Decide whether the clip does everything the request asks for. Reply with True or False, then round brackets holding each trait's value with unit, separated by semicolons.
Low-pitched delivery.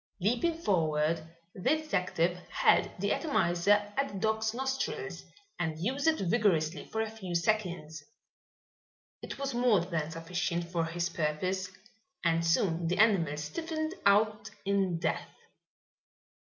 False (185 Hz)